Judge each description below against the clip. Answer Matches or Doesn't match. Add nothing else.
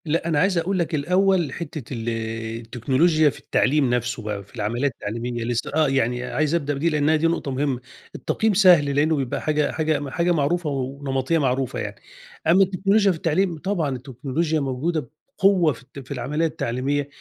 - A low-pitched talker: Doesn't match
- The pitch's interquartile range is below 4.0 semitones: Doesn't match